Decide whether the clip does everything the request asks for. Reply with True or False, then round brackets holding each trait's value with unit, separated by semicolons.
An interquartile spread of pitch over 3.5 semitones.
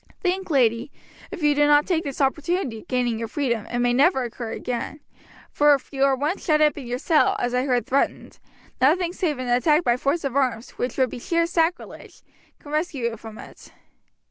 True (4.1 semitones)